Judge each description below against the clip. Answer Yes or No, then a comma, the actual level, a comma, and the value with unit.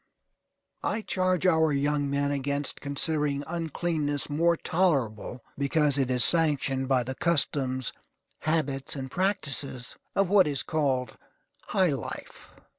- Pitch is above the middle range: No, medium, 145 Hz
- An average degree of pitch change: Yes, average, 3.4 semitones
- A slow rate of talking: Yes, slow, 120 wpm